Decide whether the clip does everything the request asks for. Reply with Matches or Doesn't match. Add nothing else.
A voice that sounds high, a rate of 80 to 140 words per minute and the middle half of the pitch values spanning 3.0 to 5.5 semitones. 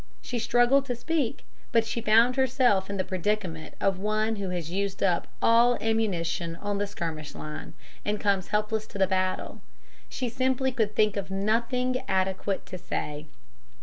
Doesn't match